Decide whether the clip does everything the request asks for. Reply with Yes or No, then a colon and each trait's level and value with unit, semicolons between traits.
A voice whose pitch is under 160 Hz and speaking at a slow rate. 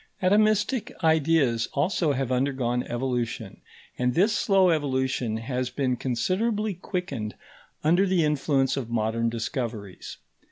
Yes: low, 135 Hz; slow, 115 wpm